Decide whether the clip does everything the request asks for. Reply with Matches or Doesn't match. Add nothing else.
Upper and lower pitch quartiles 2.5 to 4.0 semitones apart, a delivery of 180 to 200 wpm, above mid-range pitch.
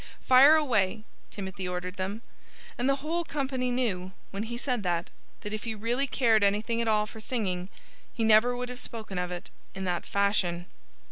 Doesn't match